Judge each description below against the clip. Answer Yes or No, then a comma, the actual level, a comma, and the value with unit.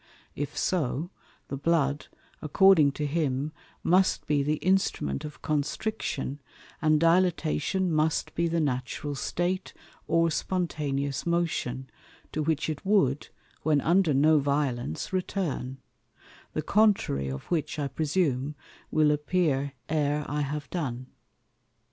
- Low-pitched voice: No, medium, 150 Hz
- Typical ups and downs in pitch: Yes, average, 3.4 semitones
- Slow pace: Yes, slow, 120 wpm